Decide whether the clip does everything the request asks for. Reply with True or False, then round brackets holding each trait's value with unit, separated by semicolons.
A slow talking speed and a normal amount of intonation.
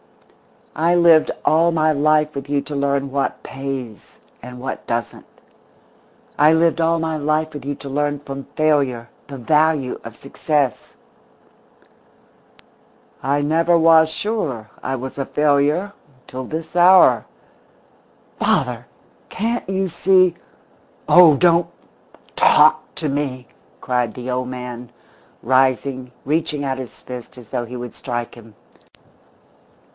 True (130 wpm; 3.9 semitones)